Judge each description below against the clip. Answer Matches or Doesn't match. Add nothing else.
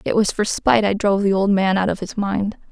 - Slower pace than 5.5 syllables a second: Doesn't match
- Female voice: Matches